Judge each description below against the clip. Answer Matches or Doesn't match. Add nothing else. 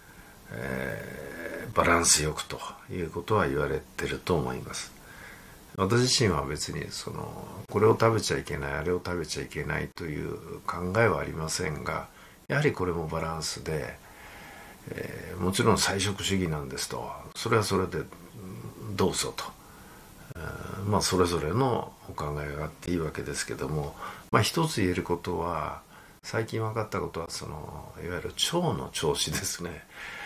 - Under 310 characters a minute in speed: Doesn't match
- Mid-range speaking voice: Doesn't match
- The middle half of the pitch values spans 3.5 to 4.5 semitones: Matches